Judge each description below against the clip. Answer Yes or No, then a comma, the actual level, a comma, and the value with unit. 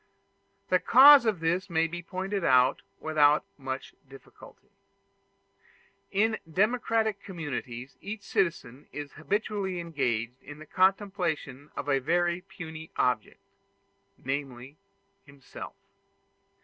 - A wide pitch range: Yes, wide, 5.8 semitones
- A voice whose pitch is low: No, medium, 165 Hz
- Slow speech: Yes, slow, 105 wpm